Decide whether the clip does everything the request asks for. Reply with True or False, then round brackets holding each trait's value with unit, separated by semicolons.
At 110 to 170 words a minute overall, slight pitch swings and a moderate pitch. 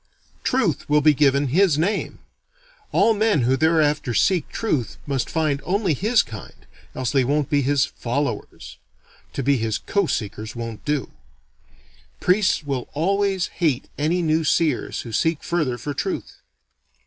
False (150 wpm; 4.7 semitones; 150 Hz)